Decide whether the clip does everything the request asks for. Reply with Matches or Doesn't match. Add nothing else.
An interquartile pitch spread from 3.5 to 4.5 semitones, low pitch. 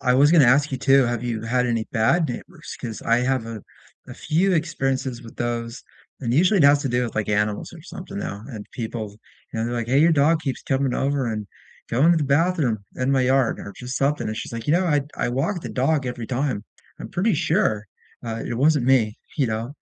Matches